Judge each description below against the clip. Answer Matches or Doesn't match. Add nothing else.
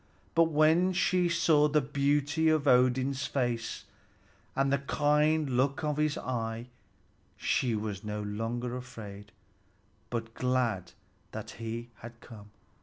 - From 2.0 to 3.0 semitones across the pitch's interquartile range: Doesn't match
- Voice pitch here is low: Matches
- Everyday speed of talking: Doesn't match